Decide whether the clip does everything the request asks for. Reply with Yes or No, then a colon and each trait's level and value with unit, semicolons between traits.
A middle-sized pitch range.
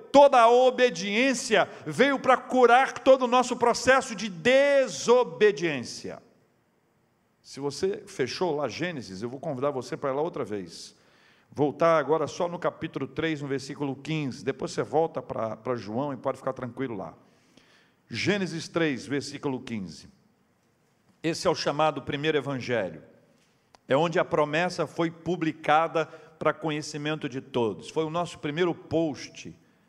No: wide, 6.3 semitones